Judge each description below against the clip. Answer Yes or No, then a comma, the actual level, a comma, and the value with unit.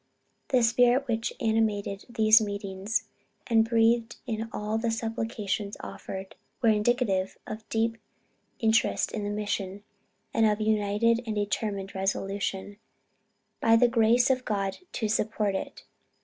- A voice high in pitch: Yes, high, 220 Hz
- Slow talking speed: Yes, slow, 130 wpm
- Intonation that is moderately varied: No, narrow, 2.0 semitones